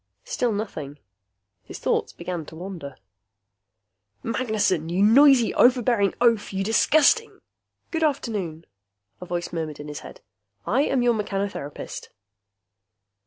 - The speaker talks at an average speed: No, slow, 120 wpm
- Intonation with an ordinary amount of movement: No, wide, 6.1 semitones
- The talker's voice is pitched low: No, high, 205 Hz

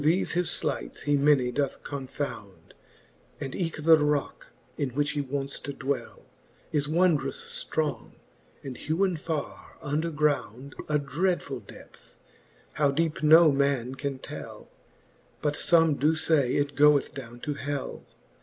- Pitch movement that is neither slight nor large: No, narrow, 2.3 semitones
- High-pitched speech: No, medium, 145 Hz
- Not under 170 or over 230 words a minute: No, average, 145 wpm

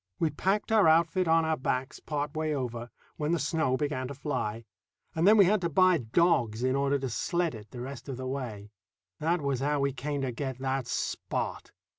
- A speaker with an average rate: No, fast, 210 wpm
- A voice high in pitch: No, medium, 140 Hz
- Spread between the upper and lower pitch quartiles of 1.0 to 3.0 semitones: No, average, 4.0 semitones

